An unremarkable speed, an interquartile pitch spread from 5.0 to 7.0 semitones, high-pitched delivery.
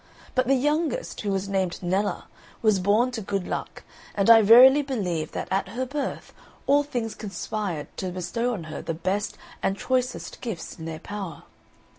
Yes: average, 175 wpm; average, 5.3 semitones; high, 205 Hz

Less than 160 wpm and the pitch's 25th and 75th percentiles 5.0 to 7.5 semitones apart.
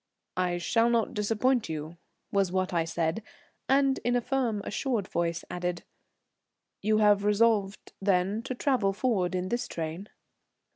No: average, 145 wpm; average, 4.5 semitones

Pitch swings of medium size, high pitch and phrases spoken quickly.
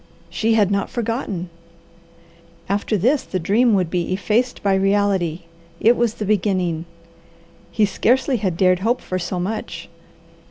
No: average, 3.6 semitones; high, 200 Hz; average, 145 wpm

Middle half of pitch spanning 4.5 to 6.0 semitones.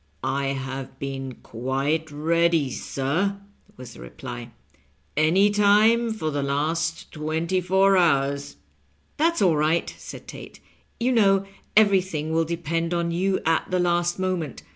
Yes: average, 5.1 semitones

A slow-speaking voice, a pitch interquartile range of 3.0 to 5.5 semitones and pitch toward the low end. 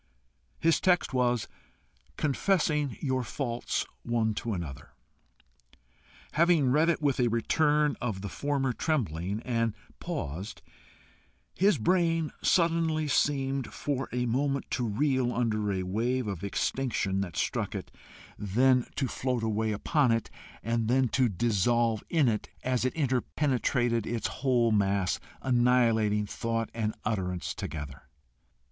Yes: slow, 125 wpm; average, 4.3 semitones; low, 120 Hz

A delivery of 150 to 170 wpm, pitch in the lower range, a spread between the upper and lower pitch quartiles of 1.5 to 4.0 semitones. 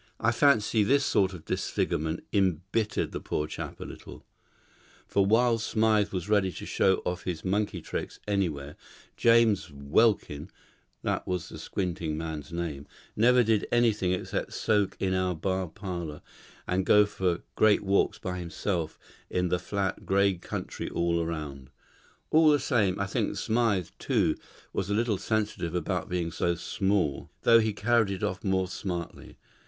Yes: average, 155 wpm; very low, 95 Hz; average, 3.7 semitones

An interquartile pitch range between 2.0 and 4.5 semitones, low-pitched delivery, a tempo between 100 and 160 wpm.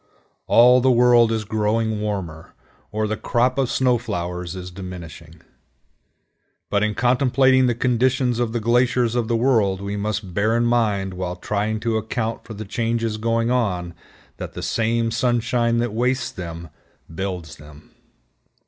Yes: average, 3.6 semitones; low, 110 Hz; average, 155 wpm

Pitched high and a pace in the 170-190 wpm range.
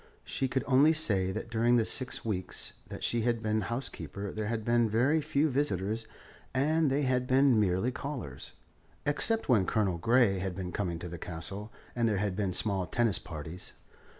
No: low, 110 Hz; average, 180 wpm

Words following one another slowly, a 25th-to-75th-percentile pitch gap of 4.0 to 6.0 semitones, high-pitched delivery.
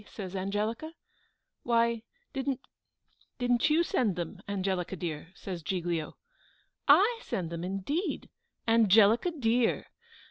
Yes: slow, 105 wpm; average, 5.1 semitones; high, 215 Hz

